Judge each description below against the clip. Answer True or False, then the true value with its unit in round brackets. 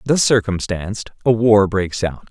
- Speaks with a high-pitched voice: False (105 Hz)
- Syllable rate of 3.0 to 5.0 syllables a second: True (4.5 syllables/s)